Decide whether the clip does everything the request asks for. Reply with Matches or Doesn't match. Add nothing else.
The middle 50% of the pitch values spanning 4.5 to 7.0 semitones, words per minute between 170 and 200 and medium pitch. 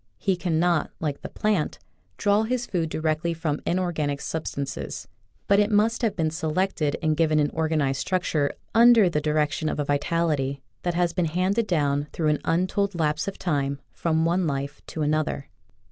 Doesn't match